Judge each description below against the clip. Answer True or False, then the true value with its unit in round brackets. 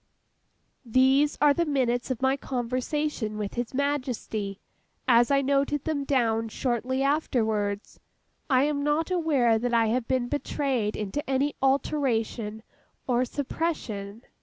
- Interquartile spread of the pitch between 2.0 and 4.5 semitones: True (3.8 semitones)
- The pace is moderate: False (130 wpm)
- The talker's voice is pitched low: False (260 Hz)